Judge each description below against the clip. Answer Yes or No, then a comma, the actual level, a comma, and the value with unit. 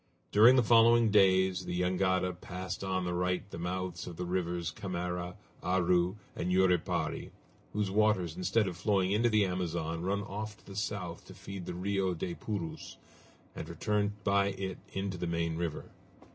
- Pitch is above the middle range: No, very low, 95 Hz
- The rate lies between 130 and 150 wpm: No, average, 170 wpm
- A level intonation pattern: Yes, narrow, 2.2 semitones